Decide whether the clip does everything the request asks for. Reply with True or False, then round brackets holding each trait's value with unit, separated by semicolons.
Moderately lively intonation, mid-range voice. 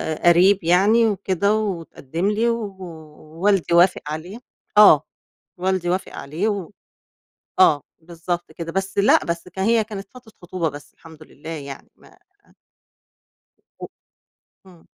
True (3.6 semitones; 180 Hz)